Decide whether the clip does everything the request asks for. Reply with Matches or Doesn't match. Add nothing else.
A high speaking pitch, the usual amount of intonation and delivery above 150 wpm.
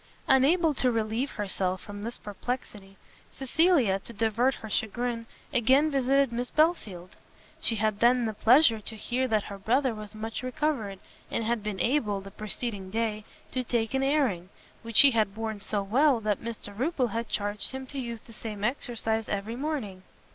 Matches